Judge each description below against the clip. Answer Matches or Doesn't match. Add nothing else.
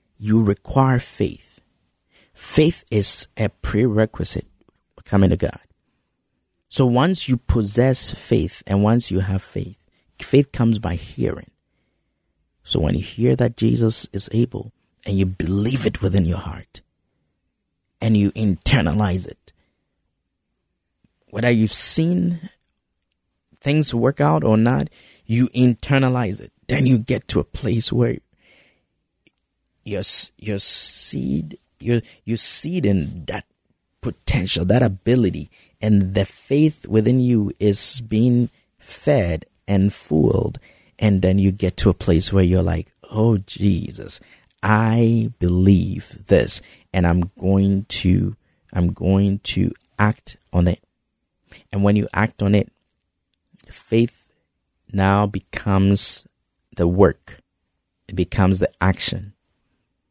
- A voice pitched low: Matches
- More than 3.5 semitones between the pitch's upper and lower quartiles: Matches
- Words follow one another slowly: Matches